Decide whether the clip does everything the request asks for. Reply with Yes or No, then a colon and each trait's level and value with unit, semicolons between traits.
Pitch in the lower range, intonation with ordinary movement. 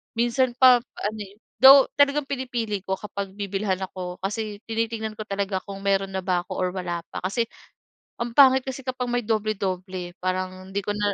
No: high, 205 Hz; average, 4.0 semitones